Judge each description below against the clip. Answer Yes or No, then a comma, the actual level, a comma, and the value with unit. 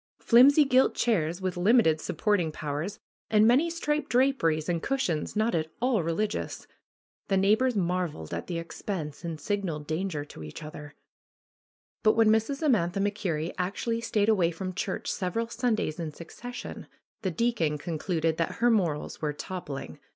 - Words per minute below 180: Yes, average, 150 wpm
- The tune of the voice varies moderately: No, wide, 6.1 semitones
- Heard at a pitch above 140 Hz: Yes, medium, 185 Hz